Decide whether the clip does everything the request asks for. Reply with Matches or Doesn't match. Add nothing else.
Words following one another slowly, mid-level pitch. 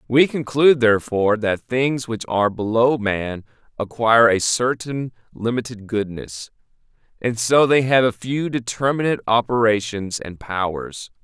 Doesn't match